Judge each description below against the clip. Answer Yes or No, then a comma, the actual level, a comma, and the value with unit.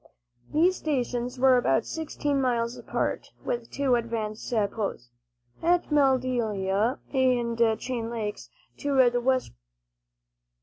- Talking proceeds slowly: Yes, slow, 105 wpm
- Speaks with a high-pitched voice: Yes, high, 245 Hz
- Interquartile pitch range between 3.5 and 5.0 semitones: No, narrow, 2.6 semitones